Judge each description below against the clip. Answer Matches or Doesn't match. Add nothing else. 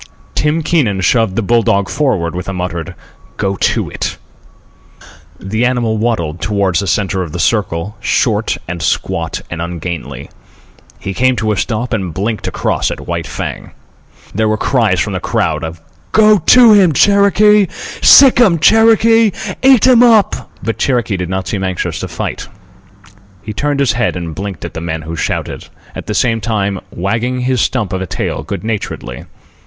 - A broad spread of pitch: Matches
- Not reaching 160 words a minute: Doesn't match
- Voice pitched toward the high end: Doesn't match